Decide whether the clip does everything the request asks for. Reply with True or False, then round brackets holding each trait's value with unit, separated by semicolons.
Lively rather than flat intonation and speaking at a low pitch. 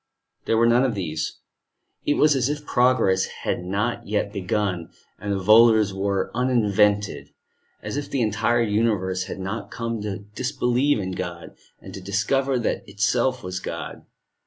False (4.0 semitones; 105 Hz)